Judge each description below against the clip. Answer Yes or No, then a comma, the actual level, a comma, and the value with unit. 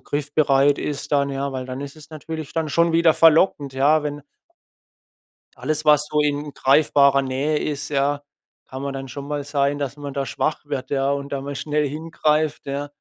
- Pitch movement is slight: Yes, narrow, 1.5 semitones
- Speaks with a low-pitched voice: No, medium, 145 Hz